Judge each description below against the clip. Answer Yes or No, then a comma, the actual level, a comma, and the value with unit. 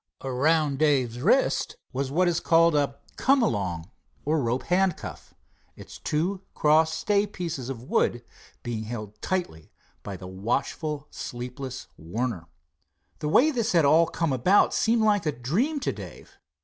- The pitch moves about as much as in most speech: No, wide, 6.4 semitones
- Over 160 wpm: No, average, 150 wpm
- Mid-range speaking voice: Yes, medium, 150 Hz